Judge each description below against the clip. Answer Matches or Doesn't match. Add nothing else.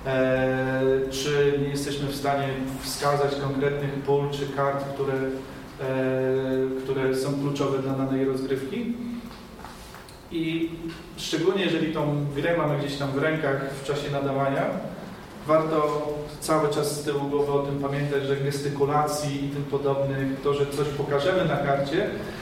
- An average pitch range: Doesn't match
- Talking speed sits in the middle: Matches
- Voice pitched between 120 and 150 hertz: Matches